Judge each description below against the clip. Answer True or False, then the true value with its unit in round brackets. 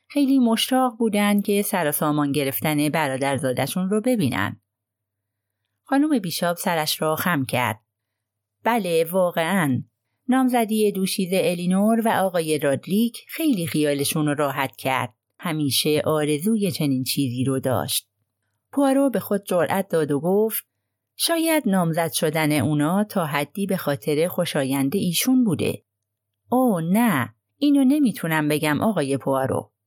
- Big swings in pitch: True (7.4 semitones)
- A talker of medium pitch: True (160 Hz)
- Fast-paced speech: False (120 wpm)